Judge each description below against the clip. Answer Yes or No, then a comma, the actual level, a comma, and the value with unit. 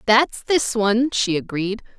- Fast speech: No, average, 150 wpm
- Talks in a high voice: Yes, high, 225 Hz